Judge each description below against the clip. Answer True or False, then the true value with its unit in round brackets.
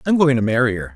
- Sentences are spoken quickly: True (315 wpm)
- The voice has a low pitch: True (125 Hz)